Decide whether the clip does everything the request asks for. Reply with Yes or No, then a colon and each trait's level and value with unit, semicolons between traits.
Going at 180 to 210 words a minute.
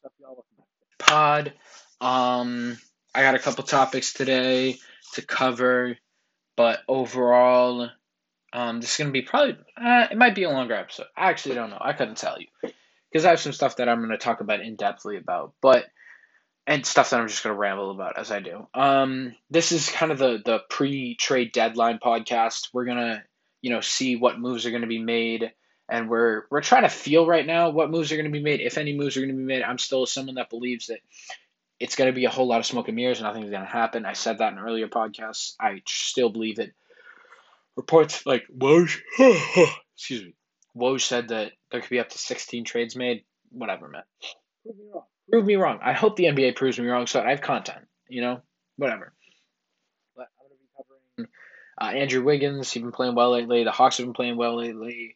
Yes: average, 200 wpm